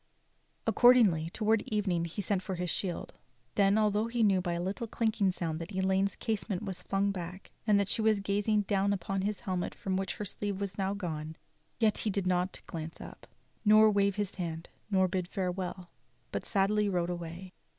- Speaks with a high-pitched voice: Yes, high, 195 Hz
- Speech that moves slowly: No, average, 190 wpm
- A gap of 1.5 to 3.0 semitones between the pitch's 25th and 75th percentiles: Yes, narrow, 2.5 semitones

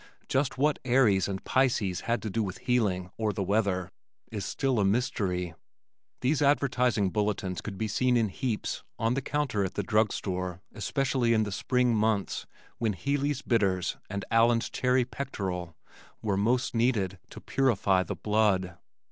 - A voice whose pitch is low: Yes, low, 110 Hz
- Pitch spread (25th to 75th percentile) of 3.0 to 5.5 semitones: Yes, average, 4.5 semitones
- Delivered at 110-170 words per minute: Yes, average, 160 wpm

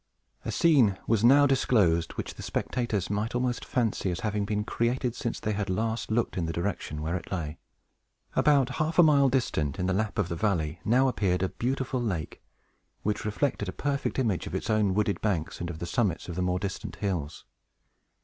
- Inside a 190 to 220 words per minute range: Yes, average, 200 wpm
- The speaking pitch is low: Yes, low, 105 Hz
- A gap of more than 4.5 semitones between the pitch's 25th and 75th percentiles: Yes, average, 5.1 semitones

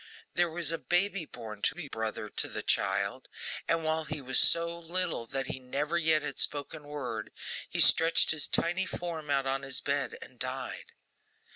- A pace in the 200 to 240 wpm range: No, average, 185 wpm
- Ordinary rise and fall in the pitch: Yes, average, 3.9 semitones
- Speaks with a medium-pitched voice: Yes, medium, 150 Hz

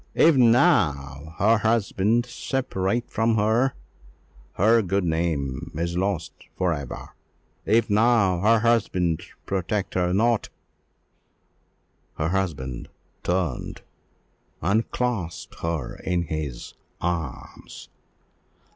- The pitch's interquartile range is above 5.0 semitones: Yes, wide, 5.4 semitones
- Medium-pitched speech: No, very low, 95 Hz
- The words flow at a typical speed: No, slow, 100 wpm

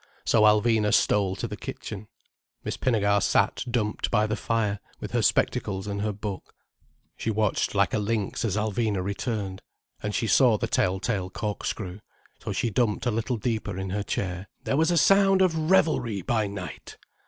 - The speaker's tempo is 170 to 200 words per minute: Yes, average, 175 wpm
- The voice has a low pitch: Yes, low, 105 Hz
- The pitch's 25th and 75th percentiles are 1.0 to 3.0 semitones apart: Yes, narrow, 2.6 semitones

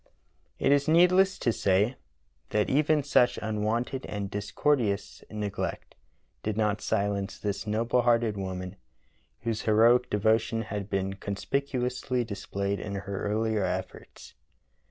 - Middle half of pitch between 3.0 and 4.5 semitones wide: Yes, average, 3.5 semitones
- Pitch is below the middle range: Yes, low, 110 Hz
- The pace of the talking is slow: Yes, slow, 120 wpm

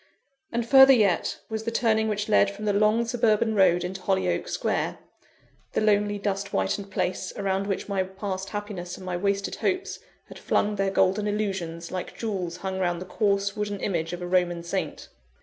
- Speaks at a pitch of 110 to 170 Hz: No, high, 200 Hz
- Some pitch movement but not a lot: No, narrow, 2.3 semitones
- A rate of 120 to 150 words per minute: No, average, 185 wpm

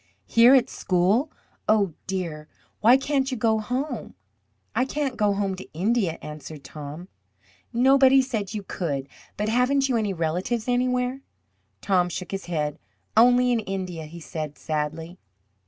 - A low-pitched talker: No, high, 205 Hz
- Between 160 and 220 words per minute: No, average, 145 wpm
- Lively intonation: Yes, wide, 6.7 semitones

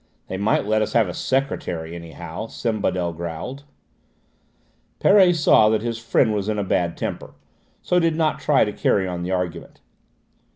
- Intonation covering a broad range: Yes, wide, 6.0 semitones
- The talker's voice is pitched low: Yes, low, 105 Hz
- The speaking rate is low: No, average, 165 wpm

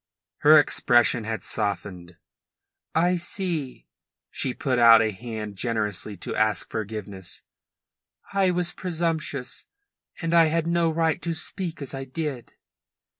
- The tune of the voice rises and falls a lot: Yes, wide, 7.3 semitones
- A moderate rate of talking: No, slow, 125 wpm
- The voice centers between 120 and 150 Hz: Yes, low, 135 Hz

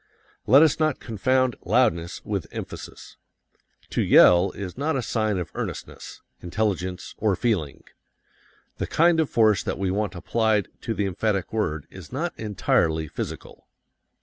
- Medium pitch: No, low, 105 Hz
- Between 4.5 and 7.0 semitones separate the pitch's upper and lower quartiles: Yes, average, 5.2 semitones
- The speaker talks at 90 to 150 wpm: Yes, average, 145 wpm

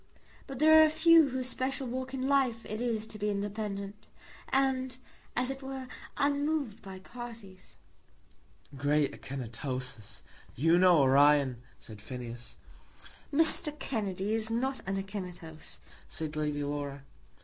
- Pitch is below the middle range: No, high, 210 Hz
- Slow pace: Yes, slow, 130 wpm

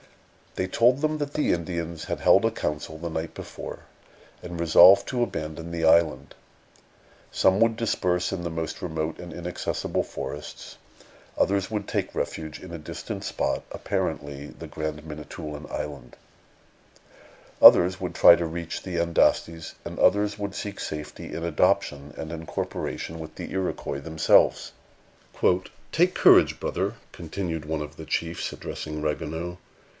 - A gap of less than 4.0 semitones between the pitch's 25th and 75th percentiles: Yes, average, 2.7 semitones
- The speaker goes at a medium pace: Yes, average, 145 wpm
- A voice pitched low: Yes, very low, 85 Hz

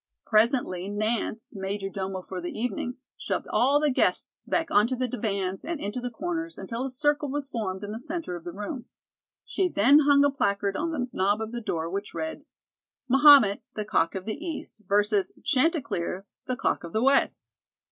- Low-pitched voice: No, high, 225 Hz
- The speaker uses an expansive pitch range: Yes, wide, 6.0 semitones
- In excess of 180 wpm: Yes, average, 190 wpm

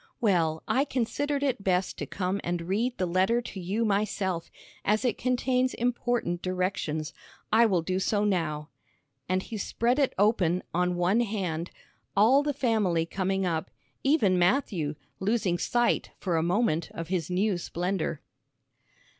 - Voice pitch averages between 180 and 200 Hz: Yes, high, 190 Hz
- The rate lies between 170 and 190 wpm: No, average, 150 wpm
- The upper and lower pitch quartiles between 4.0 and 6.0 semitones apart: Yes, average, 4.9 semitones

